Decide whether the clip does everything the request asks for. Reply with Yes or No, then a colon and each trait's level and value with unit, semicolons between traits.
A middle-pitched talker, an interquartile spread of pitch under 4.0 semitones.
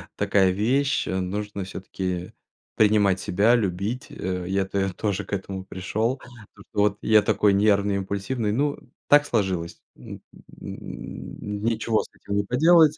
No: low, 100 Hz; average, 2.8 semitones